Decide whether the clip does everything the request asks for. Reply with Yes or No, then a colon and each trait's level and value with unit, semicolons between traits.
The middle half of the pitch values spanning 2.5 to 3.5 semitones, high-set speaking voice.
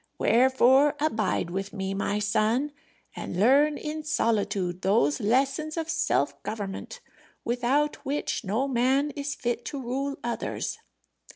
No: wide, 5.4 semitones; high, 245 Hz